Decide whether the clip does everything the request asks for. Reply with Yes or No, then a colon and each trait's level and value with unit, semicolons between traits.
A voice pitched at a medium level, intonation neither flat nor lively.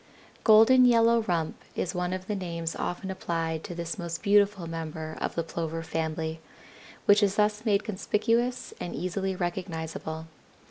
Yes: medium, 180 Hz; average, 4.1 semitones